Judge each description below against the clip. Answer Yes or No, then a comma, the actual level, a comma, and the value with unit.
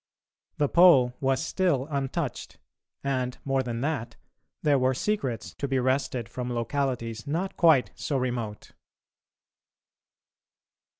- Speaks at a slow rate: Yes, slow, 115 wpm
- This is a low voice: Yes, low, 130 Hz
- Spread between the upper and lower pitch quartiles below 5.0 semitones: Yes, narrow, 2.6 semitones